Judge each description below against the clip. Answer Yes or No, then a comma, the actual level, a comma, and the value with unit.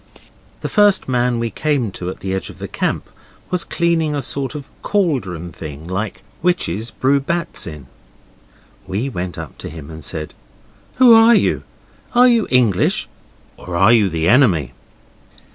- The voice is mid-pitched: No, low, 120 Hz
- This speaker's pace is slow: No, average, 160 wpm